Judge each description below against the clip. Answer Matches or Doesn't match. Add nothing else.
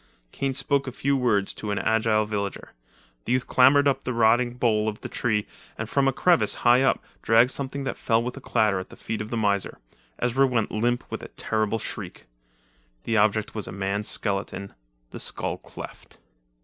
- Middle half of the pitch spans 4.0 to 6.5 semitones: Doesn't match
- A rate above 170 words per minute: Matches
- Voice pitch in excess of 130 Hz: Doesn't match